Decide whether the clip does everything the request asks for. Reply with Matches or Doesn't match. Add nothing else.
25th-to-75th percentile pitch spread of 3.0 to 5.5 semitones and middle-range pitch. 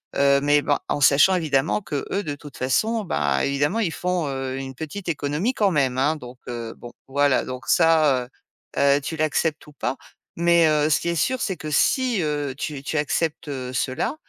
Matches